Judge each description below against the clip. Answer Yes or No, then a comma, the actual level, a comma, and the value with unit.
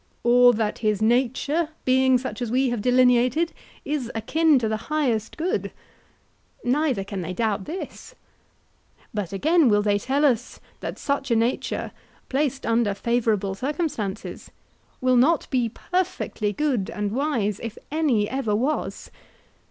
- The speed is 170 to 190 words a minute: No, average, 140 wpm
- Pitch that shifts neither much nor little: Yes, average, 4.6 semitones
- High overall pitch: Yes, high, 245 Hz